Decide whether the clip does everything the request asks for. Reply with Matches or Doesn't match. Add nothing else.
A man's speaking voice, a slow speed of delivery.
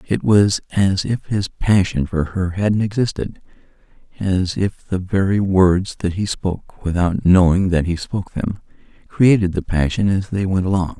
Doesn't match